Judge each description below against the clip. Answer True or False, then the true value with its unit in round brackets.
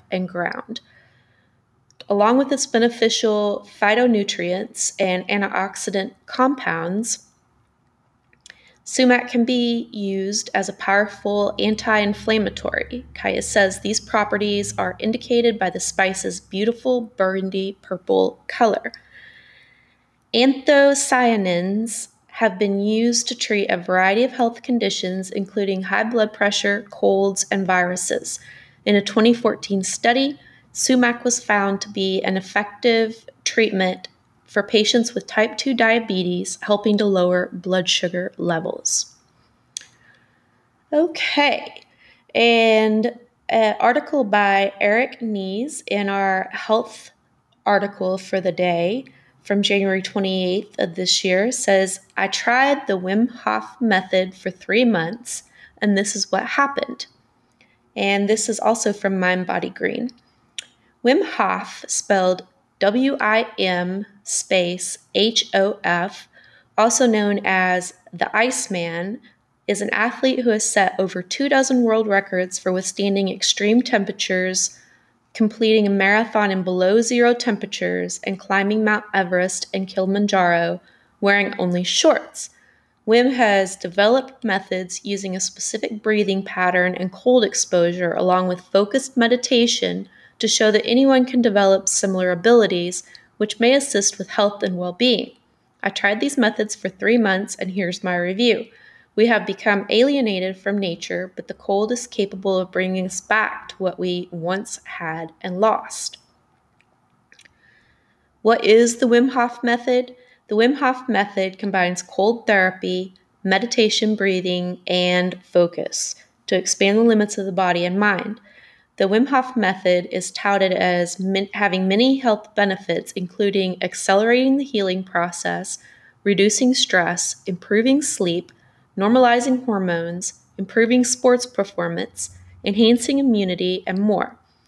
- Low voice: False (205 Hz)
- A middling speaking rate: False (125 wpm)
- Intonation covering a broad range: False (3.7 semitones)